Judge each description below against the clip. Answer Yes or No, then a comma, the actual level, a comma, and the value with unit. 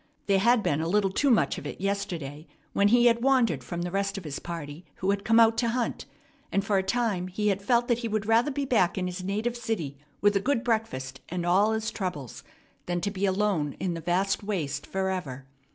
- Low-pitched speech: No, high, 195 Hz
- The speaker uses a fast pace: Yes, fast, 225 wpm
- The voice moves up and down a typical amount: Yes, average, 4.3 semitones